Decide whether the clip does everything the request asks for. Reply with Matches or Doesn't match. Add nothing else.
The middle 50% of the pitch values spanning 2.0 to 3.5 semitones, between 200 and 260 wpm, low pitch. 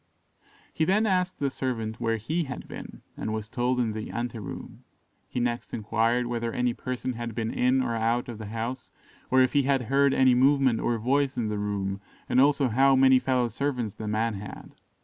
Matches